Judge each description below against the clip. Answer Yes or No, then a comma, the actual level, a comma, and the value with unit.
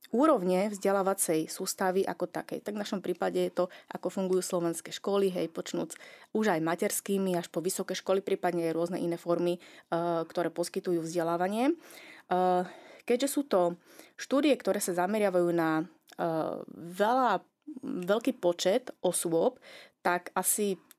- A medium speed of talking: Yes, average, 130 wpm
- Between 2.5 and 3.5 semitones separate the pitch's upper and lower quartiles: Yes, average, 2.8 semitones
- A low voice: No, medium, 185 Hz